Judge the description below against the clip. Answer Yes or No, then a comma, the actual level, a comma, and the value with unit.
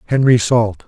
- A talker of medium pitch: No, low, 115 Hz